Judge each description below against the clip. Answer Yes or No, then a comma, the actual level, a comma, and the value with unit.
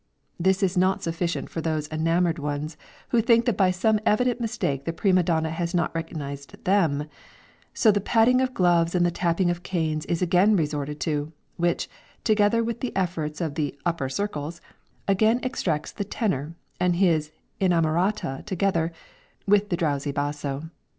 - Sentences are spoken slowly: No, average, 165 wpm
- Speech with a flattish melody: No, average, 4.1 semitones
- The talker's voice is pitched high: No, medium, 170 Hz